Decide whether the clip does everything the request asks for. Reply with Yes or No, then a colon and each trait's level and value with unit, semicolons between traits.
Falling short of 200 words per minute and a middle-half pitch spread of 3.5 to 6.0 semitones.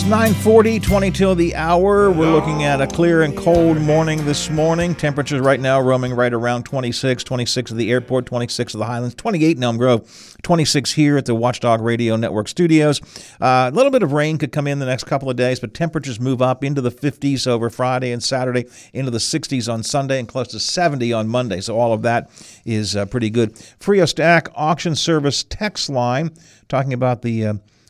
No: fast, 205 wpm; average, 4.6 semitones